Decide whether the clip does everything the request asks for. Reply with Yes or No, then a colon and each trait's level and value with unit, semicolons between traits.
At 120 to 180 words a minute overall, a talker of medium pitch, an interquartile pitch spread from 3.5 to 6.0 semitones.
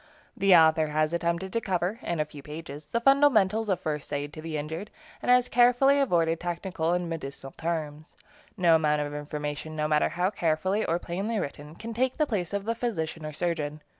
No: average, 195 wpm; medium, 170 Hz; average, 4.8 semitones